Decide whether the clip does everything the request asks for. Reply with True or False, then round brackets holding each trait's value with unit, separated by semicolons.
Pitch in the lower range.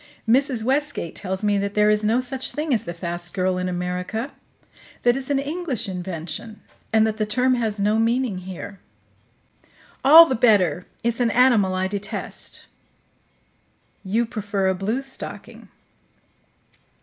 False (215 Hz)